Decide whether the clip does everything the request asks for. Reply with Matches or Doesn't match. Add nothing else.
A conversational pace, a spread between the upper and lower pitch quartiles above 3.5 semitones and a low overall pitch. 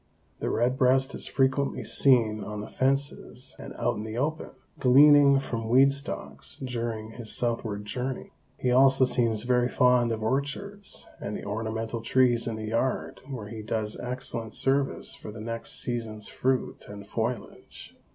Doesn't match